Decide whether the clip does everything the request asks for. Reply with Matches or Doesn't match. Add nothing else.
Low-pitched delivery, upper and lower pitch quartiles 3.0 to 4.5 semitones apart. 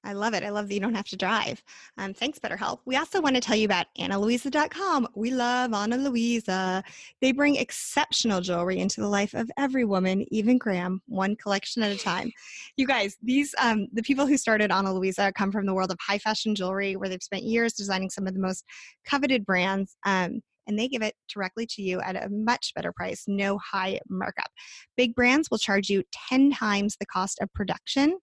Doesn't match